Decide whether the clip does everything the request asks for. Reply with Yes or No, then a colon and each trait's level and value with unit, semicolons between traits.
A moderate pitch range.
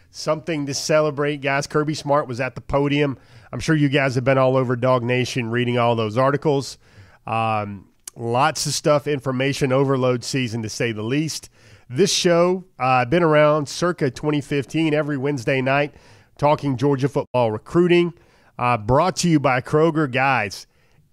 Yes: average, 3.6 semitones